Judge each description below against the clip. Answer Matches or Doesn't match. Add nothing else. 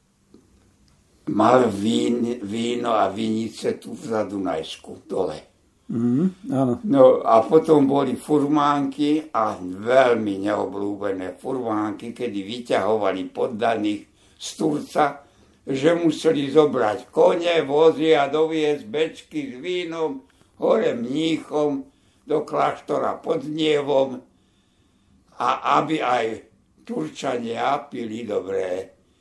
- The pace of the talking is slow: Matches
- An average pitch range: Doesn't match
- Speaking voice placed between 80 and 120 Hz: Doesn't match